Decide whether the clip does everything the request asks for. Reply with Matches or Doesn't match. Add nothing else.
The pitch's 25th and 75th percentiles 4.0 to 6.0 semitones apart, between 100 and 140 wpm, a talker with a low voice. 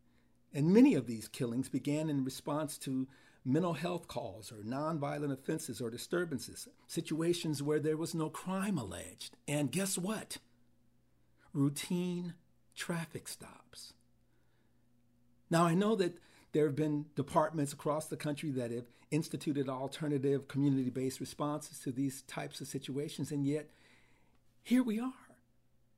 Doesn't match